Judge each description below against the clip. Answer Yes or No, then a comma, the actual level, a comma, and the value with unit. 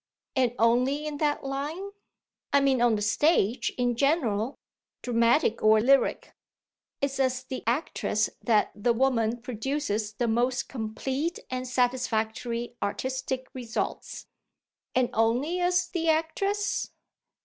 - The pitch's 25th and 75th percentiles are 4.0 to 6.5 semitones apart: No, average, 3.5 semitones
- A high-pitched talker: Yes, very high, 255 Hz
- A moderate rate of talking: No, slow, 120 wpm